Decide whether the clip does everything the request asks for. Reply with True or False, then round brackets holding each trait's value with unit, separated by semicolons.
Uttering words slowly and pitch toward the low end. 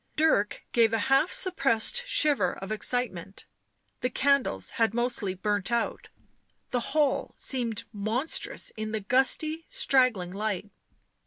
False (125 wpm; 235 Hz)